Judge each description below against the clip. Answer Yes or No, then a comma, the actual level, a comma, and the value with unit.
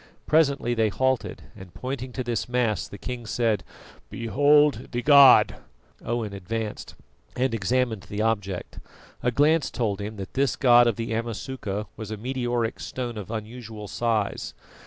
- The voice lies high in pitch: No, low, 115 Hz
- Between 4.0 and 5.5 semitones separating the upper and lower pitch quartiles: No, average, 3.1 semitones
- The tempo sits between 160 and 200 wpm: No, average, 150 wpm